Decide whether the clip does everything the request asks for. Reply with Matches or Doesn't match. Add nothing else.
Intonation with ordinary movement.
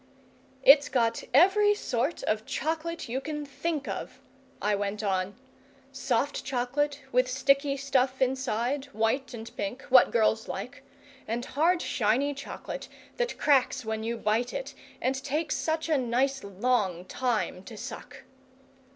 Matches